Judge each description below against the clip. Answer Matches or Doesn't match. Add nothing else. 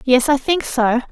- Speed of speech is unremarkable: Doesn't match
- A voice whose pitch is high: Matches